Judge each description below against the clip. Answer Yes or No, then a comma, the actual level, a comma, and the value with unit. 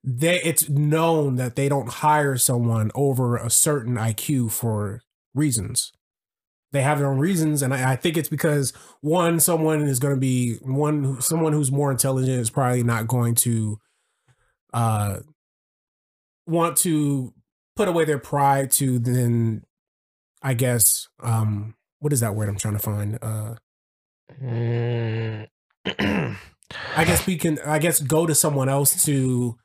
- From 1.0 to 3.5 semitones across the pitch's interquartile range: No, average, 4.5 semitones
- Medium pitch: No, low, 130 Hz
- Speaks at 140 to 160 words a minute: Yes, average, 150 wpm